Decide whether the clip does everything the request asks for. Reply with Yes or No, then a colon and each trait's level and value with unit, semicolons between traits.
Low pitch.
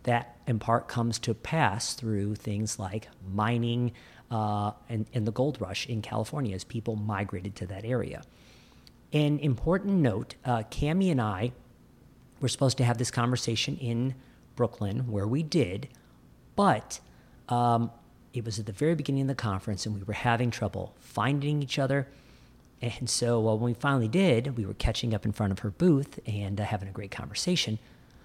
Yes: low, 120 Hz